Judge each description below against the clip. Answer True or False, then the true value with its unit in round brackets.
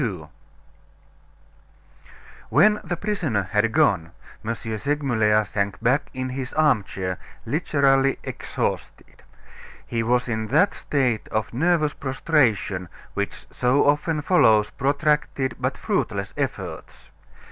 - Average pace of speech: False (105 wpm)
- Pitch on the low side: True (130 Hz)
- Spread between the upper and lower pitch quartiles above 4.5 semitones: True (5.3 semitones)